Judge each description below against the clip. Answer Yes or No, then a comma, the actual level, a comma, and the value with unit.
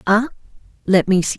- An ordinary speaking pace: Yes, average, 175 wpm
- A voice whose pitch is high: Yes, high, 195 Hz